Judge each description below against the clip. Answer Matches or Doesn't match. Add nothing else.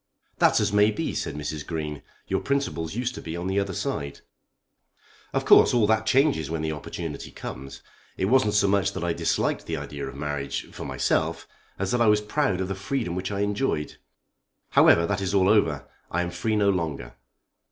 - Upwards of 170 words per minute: Matches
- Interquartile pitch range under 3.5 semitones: Doesn't match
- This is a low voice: Matches